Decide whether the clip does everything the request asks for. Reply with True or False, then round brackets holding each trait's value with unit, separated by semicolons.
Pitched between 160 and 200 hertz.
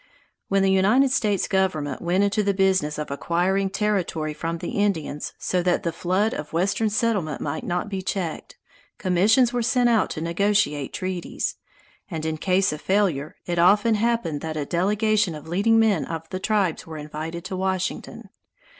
True (185 Hz)